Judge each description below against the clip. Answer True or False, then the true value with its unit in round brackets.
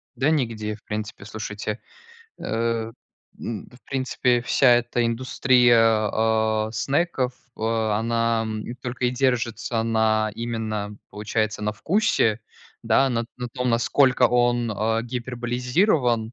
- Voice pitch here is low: True (115 Hz)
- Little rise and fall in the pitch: True (2.1 semitones)